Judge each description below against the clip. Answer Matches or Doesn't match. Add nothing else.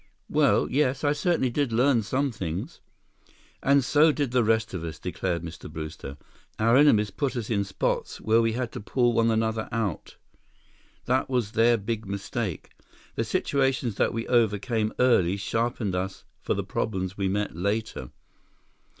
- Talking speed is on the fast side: Doesn't match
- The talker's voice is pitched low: Matches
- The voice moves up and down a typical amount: Matches